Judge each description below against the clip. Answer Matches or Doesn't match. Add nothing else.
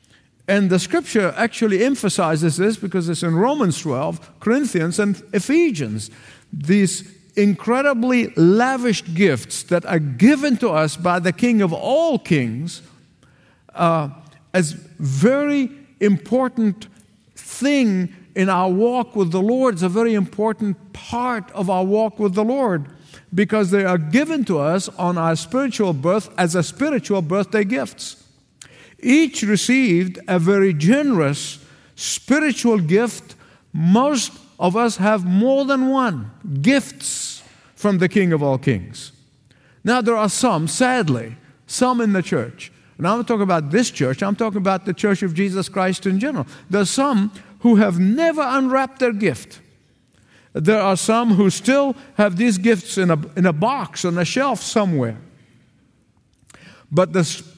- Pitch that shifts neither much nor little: Doesn't match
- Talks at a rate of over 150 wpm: Doesn't match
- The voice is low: Doesn't match